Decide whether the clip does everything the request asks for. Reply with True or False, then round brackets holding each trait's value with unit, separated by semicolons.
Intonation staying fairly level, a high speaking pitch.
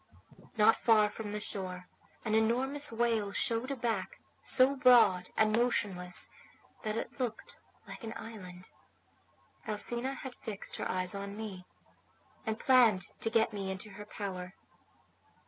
False (3.2 semitones; 220 Hz)